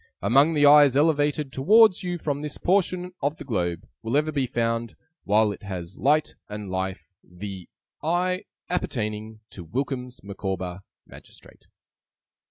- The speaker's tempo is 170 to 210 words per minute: No, average, 140 wpm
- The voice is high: No, low, 130 Hz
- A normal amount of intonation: No, wide, 6.9 semitones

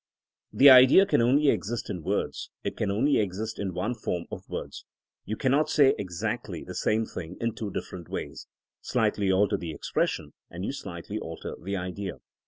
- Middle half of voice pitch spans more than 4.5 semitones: Yes, average, 5.0 semitones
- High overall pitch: No, low, 100 Hz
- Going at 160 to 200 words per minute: Yes, average, 180 wpm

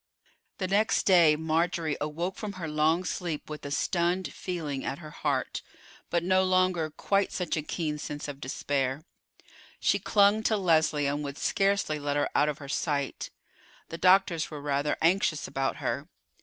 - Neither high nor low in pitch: Yes, medium, 160 Hz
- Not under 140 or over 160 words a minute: No, average, 170 wpm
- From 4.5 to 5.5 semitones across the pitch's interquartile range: No, average, 3.9 semitones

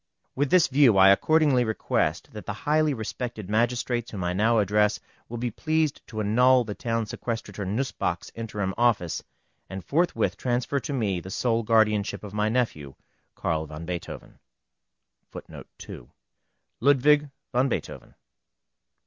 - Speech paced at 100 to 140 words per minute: Yes, slow, 135 wpm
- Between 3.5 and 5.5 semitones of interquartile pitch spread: Yes, average, 4.0 semitones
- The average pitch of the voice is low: Yes, low, 115 Hz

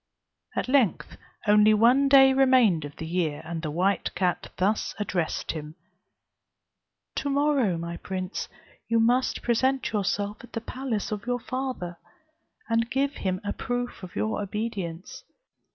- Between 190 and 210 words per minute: No, average, 145 wpm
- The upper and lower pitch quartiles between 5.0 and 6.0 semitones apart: Yes, wide, 5.6 semitones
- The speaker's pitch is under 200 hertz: No, high, 215 Hz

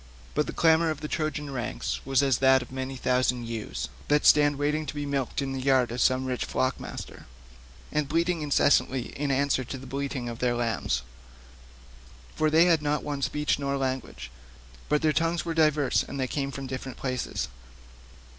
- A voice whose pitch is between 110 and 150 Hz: Yes, low, 135 Hz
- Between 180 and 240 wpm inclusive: Yes, average, 195 wpm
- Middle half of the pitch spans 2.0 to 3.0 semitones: Yes, narrow, 2.5 semitones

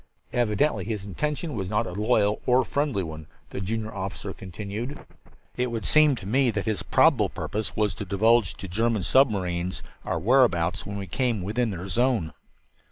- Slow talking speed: No, average, 170 wpm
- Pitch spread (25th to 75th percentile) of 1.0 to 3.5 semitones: No, average, 4.0 semitones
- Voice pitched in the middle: No, low, 105 Hz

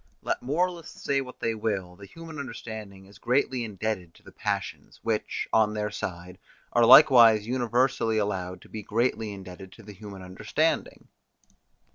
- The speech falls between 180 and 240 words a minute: No, average, 155 wpm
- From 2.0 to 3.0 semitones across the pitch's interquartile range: No, average, 3.9 semitones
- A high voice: No, low, 110 Hz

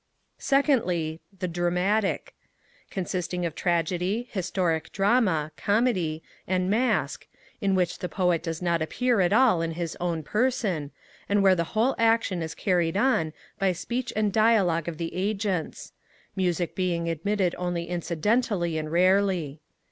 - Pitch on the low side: No, medium, 180 Hz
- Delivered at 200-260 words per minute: No, average, 140 wpm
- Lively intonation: No, average, 3.6 semitones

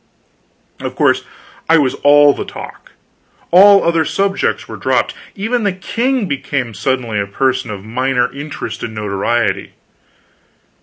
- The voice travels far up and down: Yes, wide, 7.9 semitones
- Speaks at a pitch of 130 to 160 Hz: Yes, medium, 140 Hz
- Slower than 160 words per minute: Yes, slow, 135 wpm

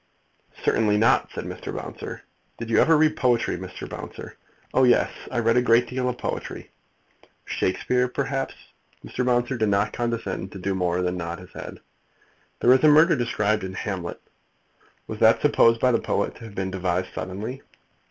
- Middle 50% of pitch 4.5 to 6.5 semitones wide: Yes, average, 4.9 semitones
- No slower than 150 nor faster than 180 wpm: Yes, average, 175 wpm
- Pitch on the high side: No, low, 115 Hz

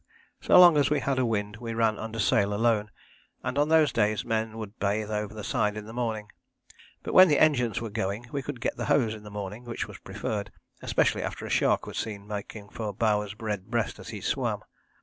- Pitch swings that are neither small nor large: No, narrow, 2.3 semitones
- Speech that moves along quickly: Yes, fast, 225 wpm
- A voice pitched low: Yes, low, 110 Hz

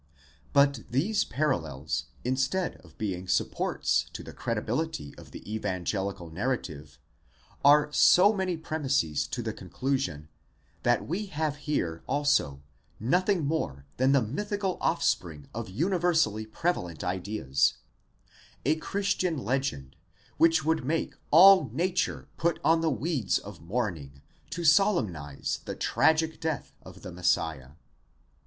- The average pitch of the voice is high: No, low, 135 Hz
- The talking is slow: Yes, slow, 125 wpm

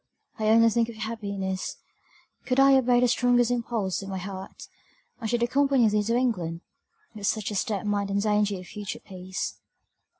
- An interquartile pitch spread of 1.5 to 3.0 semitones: No, average, 3.4 semitones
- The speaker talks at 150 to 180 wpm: Yes, average, 175 wpm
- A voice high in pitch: Yes, high, 215 Hz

